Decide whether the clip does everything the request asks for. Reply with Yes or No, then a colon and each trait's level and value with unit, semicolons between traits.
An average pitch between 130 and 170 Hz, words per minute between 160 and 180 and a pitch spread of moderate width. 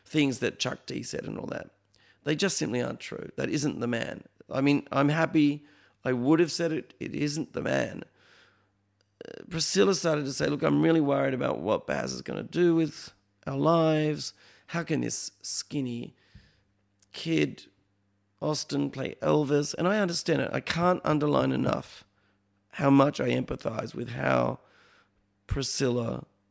No: medium, 140 Hz; average, 165 wpm; wide, 7.7 semitones